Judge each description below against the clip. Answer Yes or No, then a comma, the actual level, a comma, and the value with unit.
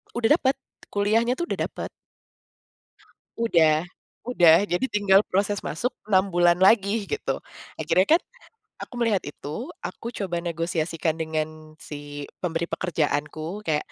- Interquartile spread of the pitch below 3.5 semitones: No, average, 4.8 semitones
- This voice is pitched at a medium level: Yes, medium, 180 Hz